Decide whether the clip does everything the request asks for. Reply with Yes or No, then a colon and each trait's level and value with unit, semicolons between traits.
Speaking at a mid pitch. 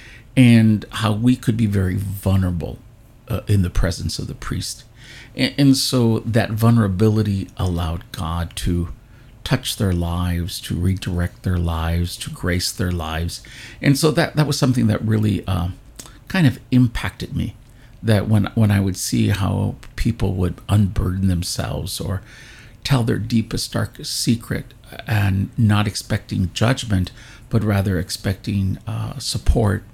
No: low, 110 Hz